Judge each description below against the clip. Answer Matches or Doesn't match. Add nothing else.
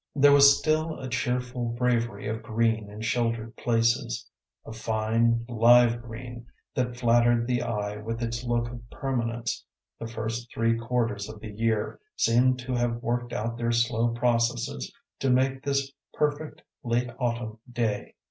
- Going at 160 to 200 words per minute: Doesn't match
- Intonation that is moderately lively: Doesn't match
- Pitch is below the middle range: Matches